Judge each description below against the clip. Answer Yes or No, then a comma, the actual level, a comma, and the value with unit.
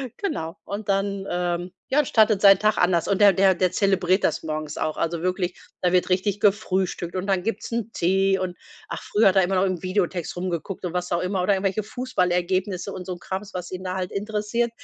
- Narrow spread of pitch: Yes, narrow, 2.0 semitones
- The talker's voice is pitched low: No, high, 190 Hz